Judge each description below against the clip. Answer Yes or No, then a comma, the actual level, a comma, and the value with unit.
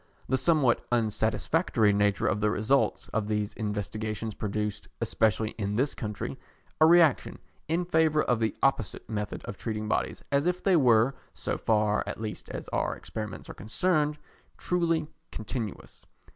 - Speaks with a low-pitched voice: Yes, low, 110 Hz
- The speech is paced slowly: No, average, 150 wpm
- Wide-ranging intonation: Yes, wide, 6.0 semitones